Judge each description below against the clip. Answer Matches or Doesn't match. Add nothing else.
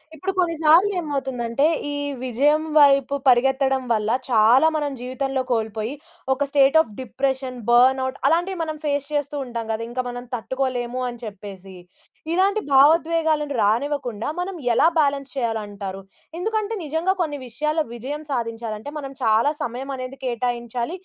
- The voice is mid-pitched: Doesn't match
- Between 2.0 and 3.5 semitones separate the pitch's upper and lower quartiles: Doesn't match